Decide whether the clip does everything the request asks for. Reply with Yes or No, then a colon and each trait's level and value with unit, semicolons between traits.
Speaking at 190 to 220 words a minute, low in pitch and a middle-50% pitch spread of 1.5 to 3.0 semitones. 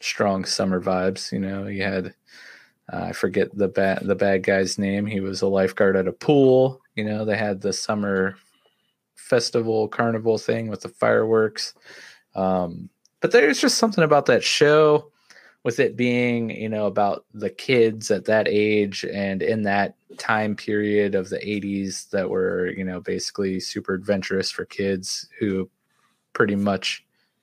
No: average, 160 wpm; low, 100 Hz; narrow, 2.5 semitones